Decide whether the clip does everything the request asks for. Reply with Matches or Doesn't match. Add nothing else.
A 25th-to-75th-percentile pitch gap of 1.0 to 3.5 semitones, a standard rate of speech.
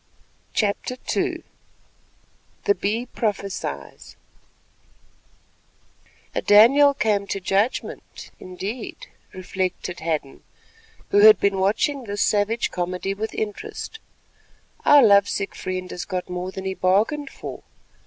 Doesn't match